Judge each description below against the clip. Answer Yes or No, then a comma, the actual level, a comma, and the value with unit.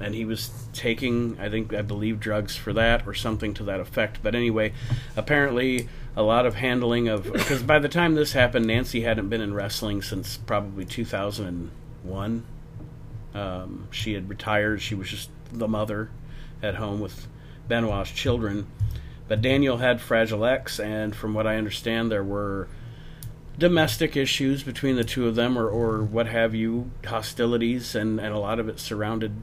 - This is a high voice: No, low, 115 Hz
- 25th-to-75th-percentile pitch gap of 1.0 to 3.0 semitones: Yes, average, 2.7 semitones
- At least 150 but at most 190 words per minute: Yes, average, 170 wpm